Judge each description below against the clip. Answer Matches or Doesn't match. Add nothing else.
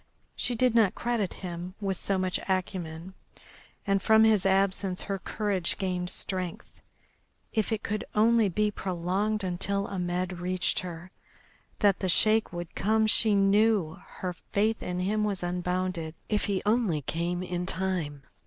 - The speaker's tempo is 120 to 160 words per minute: Matches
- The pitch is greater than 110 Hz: Matches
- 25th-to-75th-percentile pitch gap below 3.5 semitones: Matches